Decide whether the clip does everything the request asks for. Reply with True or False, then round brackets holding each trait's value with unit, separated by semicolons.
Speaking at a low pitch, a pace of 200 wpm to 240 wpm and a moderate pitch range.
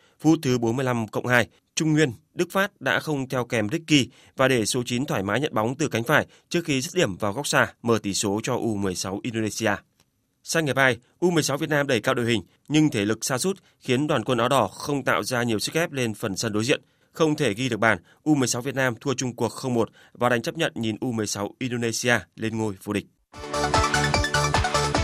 True (125 Hz; 220 wpm; 4.8 semitones)